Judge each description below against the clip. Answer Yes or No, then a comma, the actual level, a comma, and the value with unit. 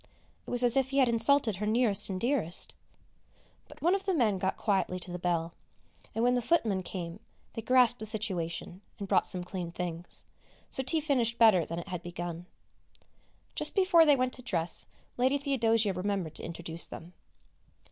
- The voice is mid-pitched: No, high, 210 Hz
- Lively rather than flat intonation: Yes, wide, 6.0 semitones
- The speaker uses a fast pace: No, average, 185 wpm